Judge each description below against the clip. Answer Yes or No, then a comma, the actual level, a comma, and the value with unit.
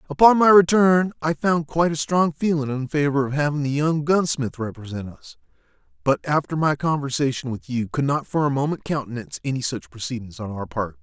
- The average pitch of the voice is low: No, medium, 145 Hz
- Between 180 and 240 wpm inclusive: Yes, average, 195 wpm